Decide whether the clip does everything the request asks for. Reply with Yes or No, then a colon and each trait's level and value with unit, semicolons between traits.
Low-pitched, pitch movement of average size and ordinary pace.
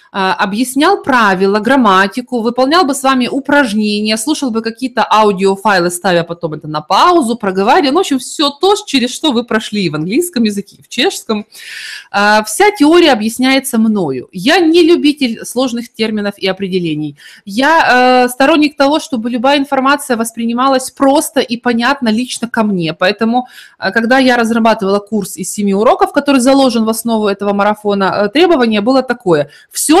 No: high, 240 Hz; average, 5.0 semitones; average, 150 wpm